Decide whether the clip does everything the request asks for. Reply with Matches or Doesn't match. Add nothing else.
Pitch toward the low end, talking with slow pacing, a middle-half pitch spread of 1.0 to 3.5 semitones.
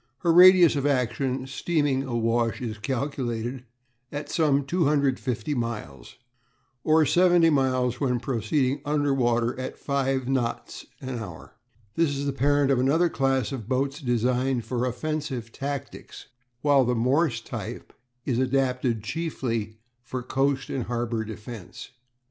Matches